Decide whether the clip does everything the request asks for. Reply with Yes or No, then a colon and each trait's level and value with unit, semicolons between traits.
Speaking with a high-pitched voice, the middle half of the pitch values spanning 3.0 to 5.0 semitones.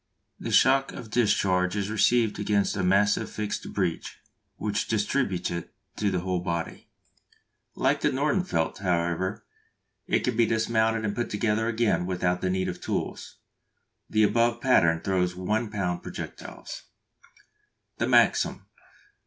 No: low, 105 Hz; average, 3.7 semitones